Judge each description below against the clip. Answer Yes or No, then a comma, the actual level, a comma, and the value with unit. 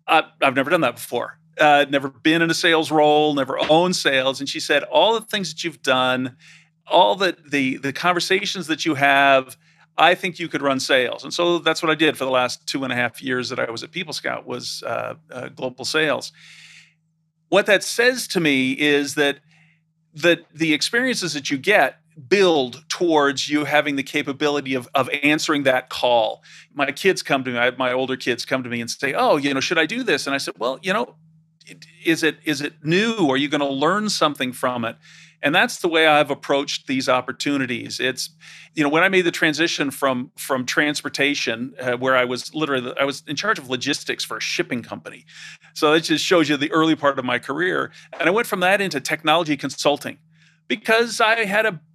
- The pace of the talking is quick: Yes, fast, 215 wpm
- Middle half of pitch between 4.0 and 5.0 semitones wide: No, average, 3.2 semitones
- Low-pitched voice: No, medium, 150 Hz